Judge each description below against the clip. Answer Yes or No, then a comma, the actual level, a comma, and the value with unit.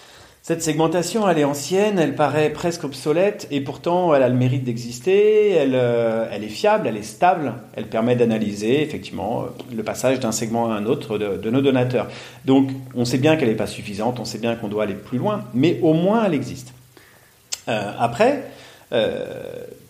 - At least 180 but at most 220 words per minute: Yes, average, 190 wpm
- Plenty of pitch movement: Yes, wide, 6.5 semitones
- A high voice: No, low, 135 Hz